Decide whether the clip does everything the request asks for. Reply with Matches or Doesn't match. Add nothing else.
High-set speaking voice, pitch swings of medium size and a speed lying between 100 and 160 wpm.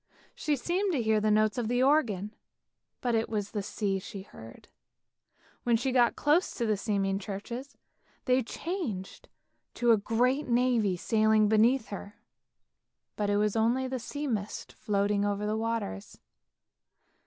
Matches